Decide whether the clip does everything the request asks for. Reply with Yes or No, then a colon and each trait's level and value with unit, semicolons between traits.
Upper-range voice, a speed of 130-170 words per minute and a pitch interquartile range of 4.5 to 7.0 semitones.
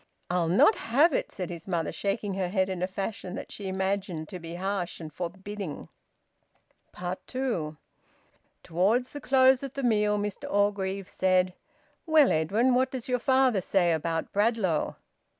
Yes: high, 195 Hz; average, 155 wpm; average, 4.9 semitones